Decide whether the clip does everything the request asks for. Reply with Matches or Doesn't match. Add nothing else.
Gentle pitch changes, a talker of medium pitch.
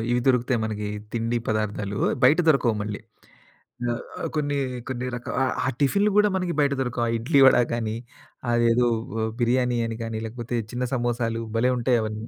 Doesn't match